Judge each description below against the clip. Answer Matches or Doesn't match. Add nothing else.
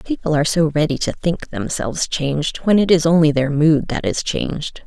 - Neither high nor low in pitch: Matches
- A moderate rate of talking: Doesn't match